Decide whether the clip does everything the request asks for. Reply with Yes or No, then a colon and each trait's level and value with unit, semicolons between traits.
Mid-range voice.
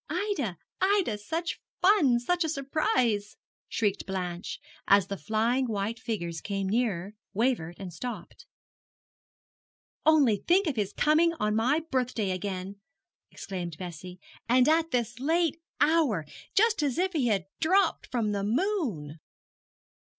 No: high, 235 Hz